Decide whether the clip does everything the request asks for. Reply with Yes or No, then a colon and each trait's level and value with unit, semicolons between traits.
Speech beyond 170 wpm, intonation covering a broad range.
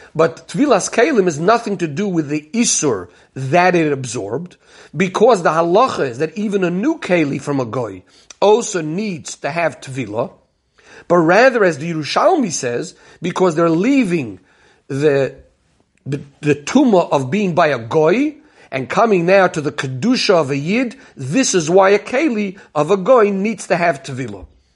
No: average, 165 wpm; wide, 5.8 semitones